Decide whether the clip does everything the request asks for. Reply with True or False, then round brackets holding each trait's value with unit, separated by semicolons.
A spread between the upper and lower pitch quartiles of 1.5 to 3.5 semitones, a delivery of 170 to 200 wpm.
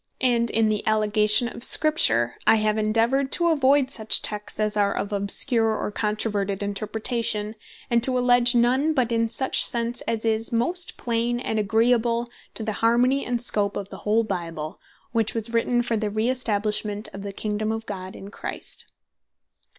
True (2.4 semitones; 175 wpm)